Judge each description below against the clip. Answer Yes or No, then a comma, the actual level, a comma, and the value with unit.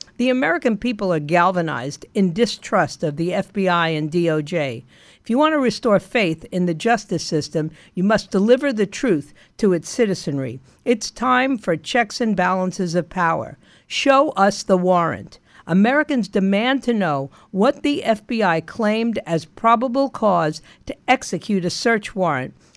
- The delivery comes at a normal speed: Yes, average, 170 wpm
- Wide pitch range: Yes, wide, 6.0 semitones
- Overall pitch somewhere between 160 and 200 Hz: Yes, high, 190 Hz